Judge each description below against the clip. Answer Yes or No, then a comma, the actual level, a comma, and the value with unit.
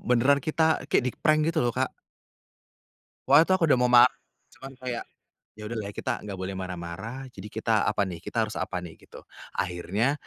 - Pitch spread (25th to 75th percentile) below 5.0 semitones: No, wide, 5.6 semitones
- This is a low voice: Yes, low, 120 Hz